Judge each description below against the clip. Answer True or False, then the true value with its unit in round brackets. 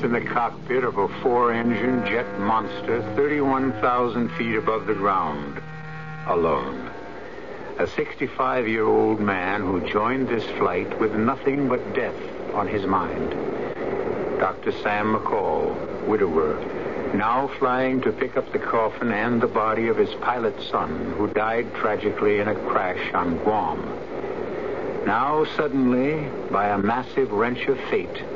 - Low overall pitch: False (155 Hz)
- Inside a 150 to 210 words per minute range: False (140 wpm)